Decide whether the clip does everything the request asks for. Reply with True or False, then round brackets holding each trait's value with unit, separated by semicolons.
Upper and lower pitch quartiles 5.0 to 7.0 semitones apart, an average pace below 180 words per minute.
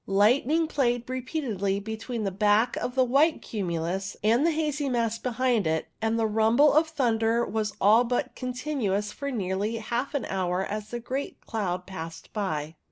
False (4.3 semitones; 170 wpm)